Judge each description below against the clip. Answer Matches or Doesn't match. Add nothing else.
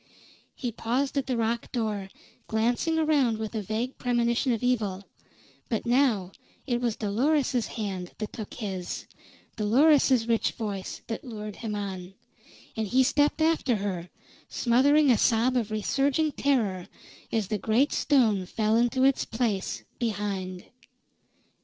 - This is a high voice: Matches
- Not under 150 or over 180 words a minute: Doesn't match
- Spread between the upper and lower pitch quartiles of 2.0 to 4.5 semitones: Matches